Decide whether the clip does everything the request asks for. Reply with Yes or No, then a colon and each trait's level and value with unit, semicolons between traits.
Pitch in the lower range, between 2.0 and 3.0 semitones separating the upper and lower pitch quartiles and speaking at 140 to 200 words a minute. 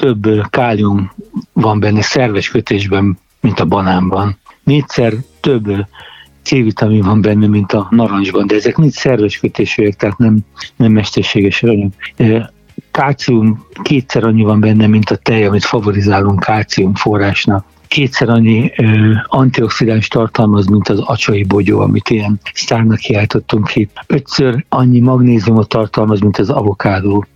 No: low, 110 Hz; narrow, 2.4 semitones; average, 130 wpm